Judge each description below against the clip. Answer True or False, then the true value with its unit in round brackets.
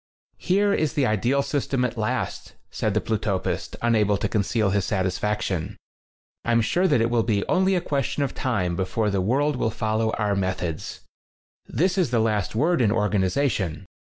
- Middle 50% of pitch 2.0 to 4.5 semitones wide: False (5.4 semitones)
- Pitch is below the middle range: True (110 Hz)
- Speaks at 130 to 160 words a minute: False (170 wpm)